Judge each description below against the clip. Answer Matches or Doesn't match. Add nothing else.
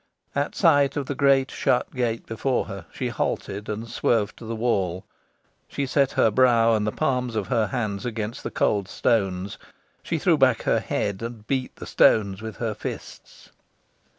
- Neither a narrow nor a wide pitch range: Matches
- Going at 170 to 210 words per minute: Matches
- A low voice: Matches